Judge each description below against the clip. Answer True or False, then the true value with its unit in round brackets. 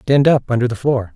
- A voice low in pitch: True (130 Hz)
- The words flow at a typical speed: False (260 wpm)